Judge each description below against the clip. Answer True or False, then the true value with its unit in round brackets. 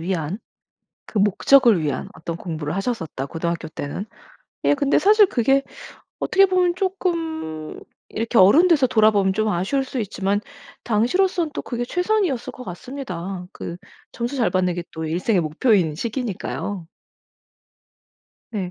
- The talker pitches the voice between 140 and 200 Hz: False (215 Hz)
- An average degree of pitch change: False (7.8 semitones)